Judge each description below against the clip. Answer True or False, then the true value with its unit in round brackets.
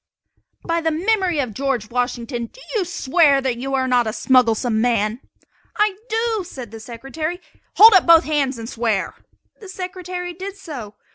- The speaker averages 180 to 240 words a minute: False (160 wpm)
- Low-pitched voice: False (275 Hz)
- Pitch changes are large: True (7.1 semitones)